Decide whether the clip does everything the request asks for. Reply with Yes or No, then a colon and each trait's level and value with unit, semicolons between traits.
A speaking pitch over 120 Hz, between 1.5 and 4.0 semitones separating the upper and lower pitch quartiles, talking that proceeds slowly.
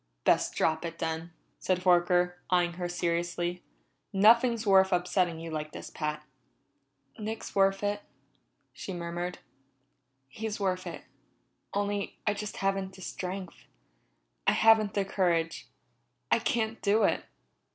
Yes: medium, 185 Hz; average, 2.8 semitones; slow, 130 wpm